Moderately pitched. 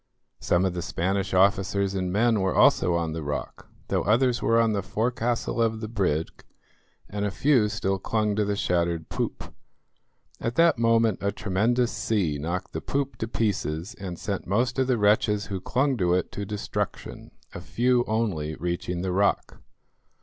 No: low, 100 Hz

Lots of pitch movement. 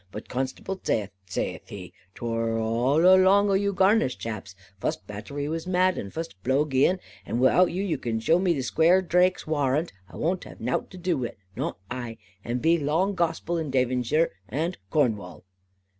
Yes: wide, 7.2 semitones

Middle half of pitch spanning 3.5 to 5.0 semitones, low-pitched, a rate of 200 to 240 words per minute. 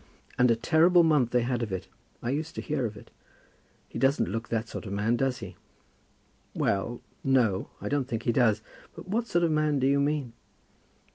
Yes: average, 4.6 semitones; low, 125 Hz; fast, 205 wpm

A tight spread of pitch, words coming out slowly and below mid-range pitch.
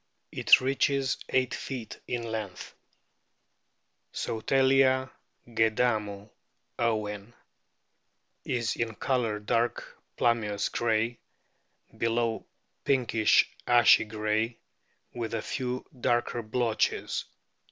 Yes: narrow, 2.3 semitones; slow, 85 wpm; low, 115 Hz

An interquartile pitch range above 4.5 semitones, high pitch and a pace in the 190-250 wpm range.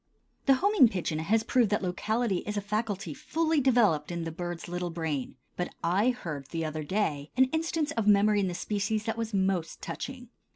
Yes: average, 5.1 semitones; high, 200 Hz; average, 195 wpm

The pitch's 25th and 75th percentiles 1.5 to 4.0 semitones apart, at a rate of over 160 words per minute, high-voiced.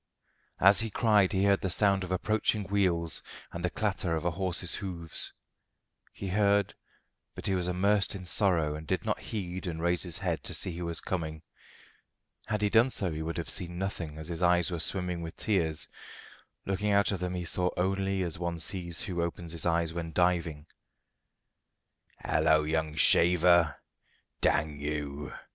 No: average, 2.8 semitones; average, 175 wpm; very low, 90 Hz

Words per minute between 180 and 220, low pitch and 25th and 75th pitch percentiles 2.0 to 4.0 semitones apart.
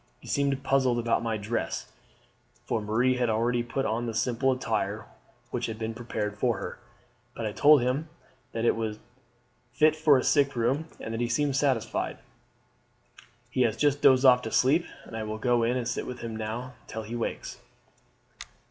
Yes: average, 185 wpm; low, 120 Hz; average, 3.0 semitones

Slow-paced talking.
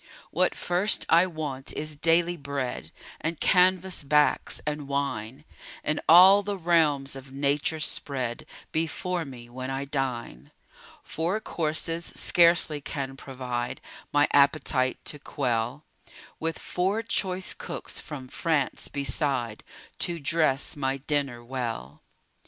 Yes: slow, 120 wpm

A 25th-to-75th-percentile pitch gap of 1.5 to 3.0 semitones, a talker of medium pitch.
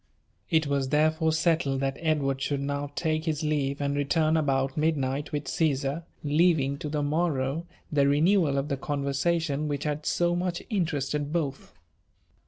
Yes: narrow, 2.4 semitones; medium, 150 Hz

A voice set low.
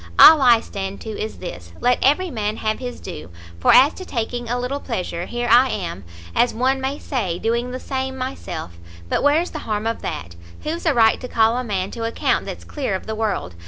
No: high, 235 Hz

